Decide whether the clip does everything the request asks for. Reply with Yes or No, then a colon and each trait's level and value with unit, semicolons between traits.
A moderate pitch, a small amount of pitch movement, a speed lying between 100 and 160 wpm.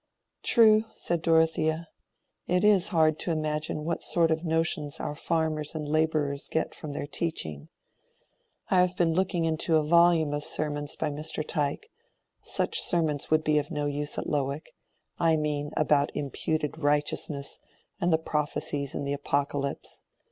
Yes: medium, 155 Hz; narrow, 1.9 semitones; average, 150 wpm